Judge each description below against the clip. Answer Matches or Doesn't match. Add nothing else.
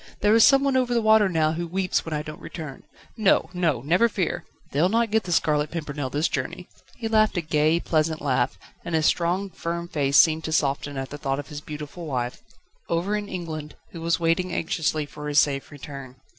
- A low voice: Doesn't match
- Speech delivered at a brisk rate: Matches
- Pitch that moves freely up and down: Doesn't match